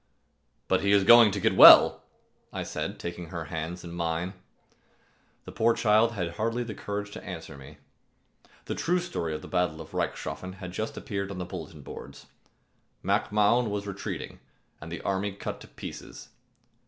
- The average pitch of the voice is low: Yes, very low, 95 Hz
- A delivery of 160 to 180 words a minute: Yes, average, 170 wpm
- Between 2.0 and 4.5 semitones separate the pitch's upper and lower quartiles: Yes, average, 3.7 semitones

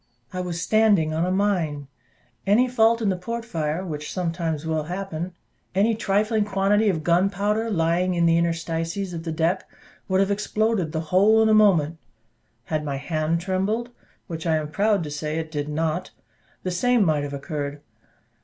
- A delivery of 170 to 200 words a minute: Yes, average, 175 wpm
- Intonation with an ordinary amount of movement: Yes, average, 4.3 semitones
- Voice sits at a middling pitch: Yes, medium, 180 Hz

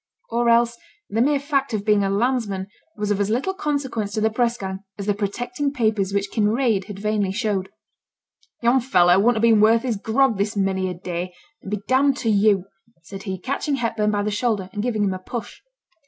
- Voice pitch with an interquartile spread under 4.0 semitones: Yes, average, 3.3 semitones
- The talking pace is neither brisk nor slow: No, fast, 215 wpm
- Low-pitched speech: No, high, 215 Hz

